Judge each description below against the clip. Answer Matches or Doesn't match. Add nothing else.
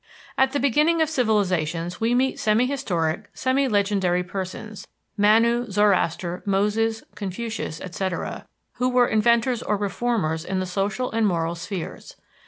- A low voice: Doesn't match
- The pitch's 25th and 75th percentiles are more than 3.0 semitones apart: Matches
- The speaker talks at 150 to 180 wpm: Doesn't match